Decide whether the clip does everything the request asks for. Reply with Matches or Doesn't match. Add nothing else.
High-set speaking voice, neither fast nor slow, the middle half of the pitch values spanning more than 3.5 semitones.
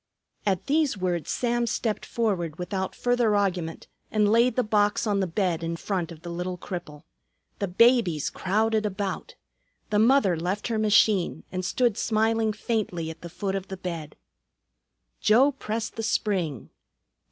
Matches